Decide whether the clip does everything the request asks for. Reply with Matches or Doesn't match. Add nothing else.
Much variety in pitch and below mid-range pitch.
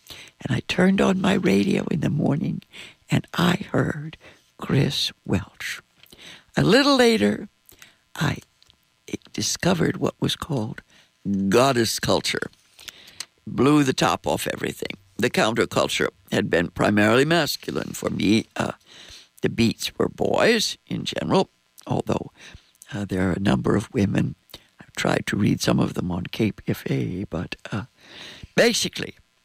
Matches